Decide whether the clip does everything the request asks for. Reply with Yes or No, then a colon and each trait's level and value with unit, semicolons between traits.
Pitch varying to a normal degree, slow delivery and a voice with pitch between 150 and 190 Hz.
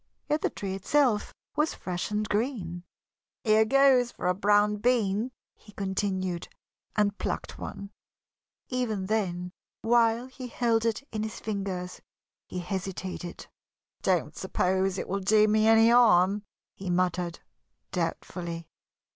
No: average, 3.4 semitones; slow, 130 wpm; high, 205 Hz